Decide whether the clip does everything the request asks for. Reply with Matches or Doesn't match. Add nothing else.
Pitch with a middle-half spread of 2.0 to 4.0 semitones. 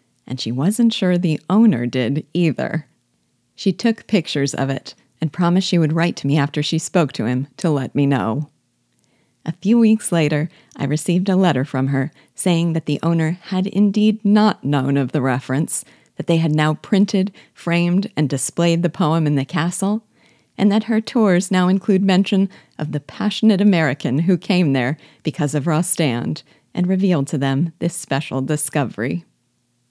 Doesn't match